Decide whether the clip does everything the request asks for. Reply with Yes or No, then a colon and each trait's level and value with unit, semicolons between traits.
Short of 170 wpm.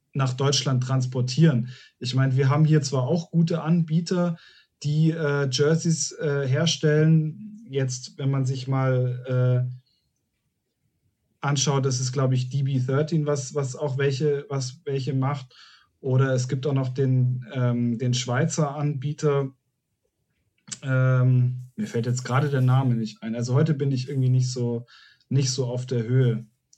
Yes: average, 150 wpm